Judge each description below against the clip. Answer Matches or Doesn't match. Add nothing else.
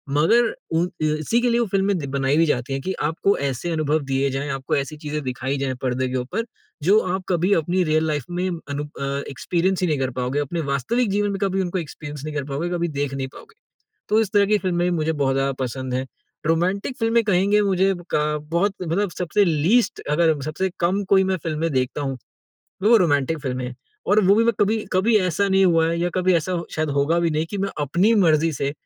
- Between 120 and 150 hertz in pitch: Doesn't match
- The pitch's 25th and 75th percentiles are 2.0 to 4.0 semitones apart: Doesn't match